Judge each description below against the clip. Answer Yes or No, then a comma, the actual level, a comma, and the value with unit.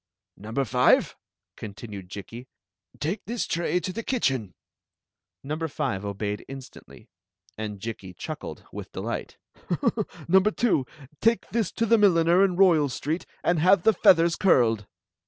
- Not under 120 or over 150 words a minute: Yes, average, 140 wpm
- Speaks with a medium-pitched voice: Yes, medium, 155 Hz